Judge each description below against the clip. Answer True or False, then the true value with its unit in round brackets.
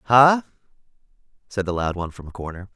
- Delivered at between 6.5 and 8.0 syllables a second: True (6.8 syllables/s)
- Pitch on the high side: False (105 Hz)